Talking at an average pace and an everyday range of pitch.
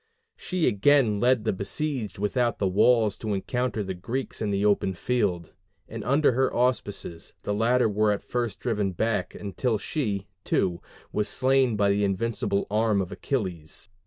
Yes: average, 160 wpm; average, 3.8 semitones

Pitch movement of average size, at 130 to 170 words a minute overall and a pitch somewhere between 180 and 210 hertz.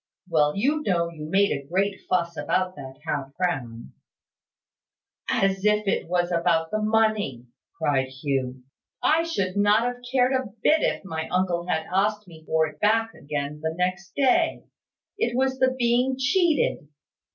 No: wide, 6.1 semitones; average, 160 wpm; medium, 185 Hz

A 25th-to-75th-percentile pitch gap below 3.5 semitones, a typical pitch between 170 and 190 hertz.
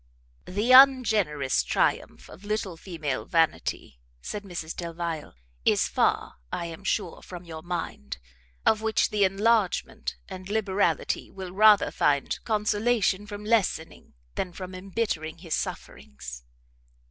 No: average, 4.5 semitones; medium, 185 Hz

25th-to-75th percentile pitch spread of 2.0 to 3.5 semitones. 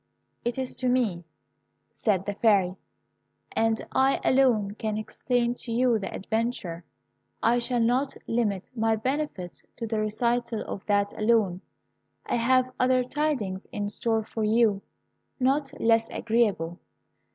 Yes: average, 3.1 semitones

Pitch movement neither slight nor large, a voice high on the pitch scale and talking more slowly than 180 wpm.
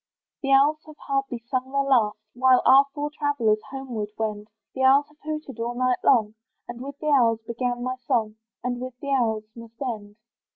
No: average, 3.2 semitones; very high, 255 Hz; average, 190 wpm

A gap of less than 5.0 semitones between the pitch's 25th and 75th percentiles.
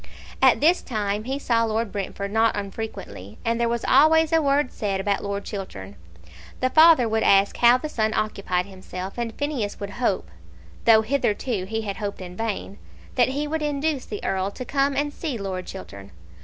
No: average, 5.3 semitones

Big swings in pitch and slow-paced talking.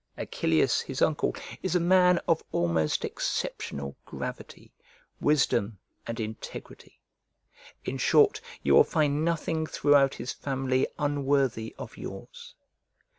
Yes: wide, 6.3 semitones; slow, 115 wpm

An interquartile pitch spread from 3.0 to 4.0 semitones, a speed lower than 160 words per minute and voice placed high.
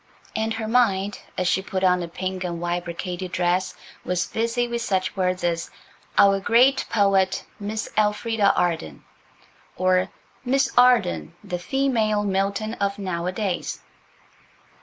Yes: average, 3.4 semitones; slow, 135 wpm; high, 195 Hz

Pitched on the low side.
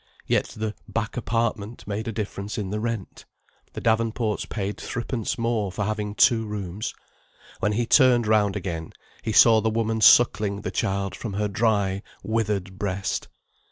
Yes: low, 105 Hz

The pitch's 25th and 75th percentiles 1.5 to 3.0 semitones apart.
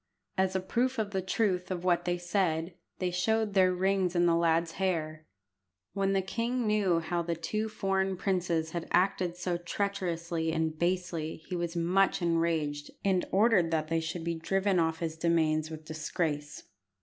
Yes: average, 2.7 semitones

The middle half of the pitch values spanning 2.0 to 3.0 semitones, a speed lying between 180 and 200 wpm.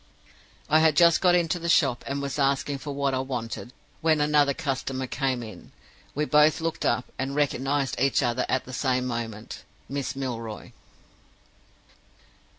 No: average, 2.7 semitones; average, 155 wpm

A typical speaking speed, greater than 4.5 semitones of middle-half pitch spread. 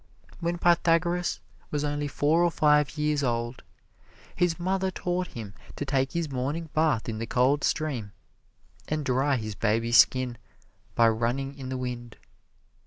Yes: average, 150 wpm; average, 5.1 semitones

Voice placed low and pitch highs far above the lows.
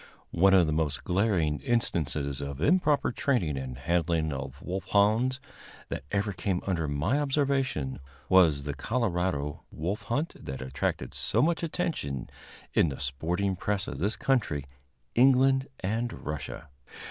Yes: very low, 90 Hz; wide, 8.4 semitones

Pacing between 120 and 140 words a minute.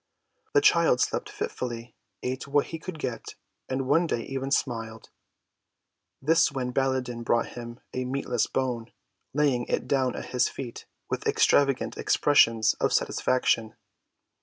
Yes: slow, 135 wpm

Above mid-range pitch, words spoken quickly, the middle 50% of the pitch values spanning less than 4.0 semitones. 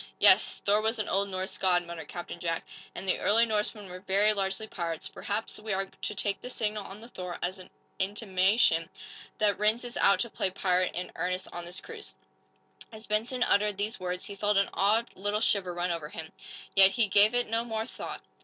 Yes: high, 200 Hz; fast, 210 wpm; average, 2.8 semitones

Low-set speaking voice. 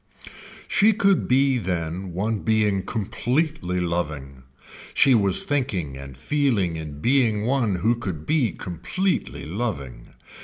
Yes: low, 100 Hz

